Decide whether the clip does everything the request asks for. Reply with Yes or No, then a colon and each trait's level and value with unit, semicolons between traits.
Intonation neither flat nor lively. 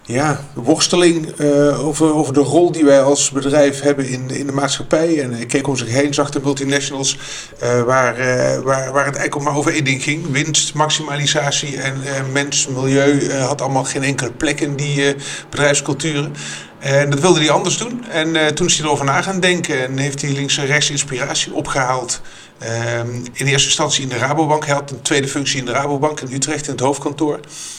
No: narrow, 1.9 semitones